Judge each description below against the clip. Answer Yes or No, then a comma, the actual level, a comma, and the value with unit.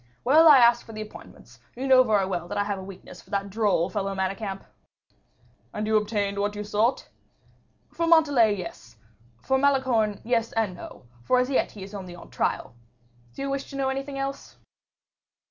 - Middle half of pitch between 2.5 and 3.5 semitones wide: No, average, 5.0 semitones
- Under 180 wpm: No, average, 195 wpm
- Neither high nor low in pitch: No, high, 215 Hz